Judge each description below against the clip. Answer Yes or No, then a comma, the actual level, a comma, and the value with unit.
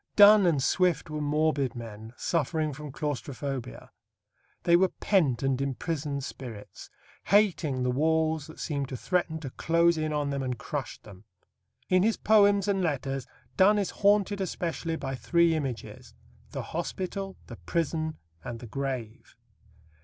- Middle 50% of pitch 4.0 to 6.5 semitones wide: Yes, average, 4.8 semitones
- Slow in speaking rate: No, average, 145 wpm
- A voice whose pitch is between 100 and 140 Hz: No, medium, 155 Hz